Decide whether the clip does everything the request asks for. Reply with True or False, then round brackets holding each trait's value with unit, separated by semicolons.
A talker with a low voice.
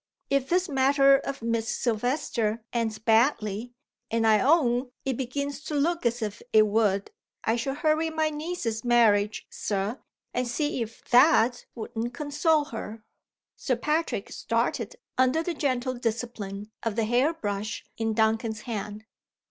False (240 Hz)